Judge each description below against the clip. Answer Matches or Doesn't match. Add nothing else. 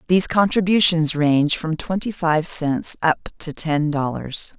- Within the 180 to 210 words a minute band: Doesn't match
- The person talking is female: Matches